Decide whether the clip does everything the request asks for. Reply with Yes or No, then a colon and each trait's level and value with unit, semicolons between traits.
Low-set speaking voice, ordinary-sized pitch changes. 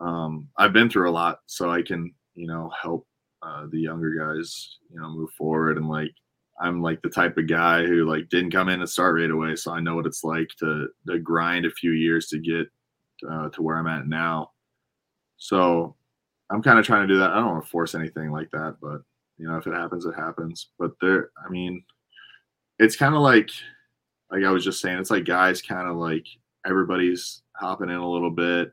No: very low, 85 Hz; narrow, 1.8 semitones